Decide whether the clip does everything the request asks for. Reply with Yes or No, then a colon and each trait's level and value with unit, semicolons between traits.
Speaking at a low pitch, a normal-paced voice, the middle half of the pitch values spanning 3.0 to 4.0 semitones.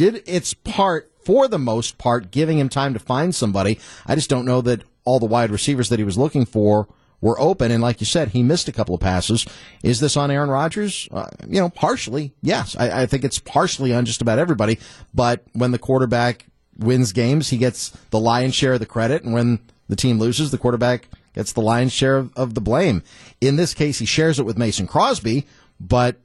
No: low, 125 Hz; fast, 220 wpm; average, 3.6 semitones